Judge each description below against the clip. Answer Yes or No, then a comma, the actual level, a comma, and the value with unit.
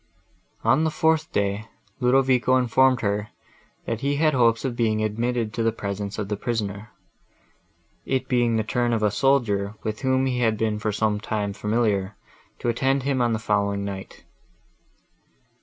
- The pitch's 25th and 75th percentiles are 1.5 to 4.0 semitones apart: Yes, average, 3.5 semitones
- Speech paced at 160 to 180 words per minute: Yes, average, 165 wpm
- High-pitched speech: No, low, 115 Hz